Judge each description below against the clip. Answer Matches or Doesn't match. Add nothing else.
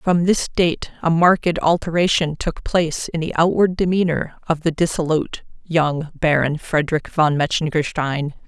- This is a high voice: Doesn't match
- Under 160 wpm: Matches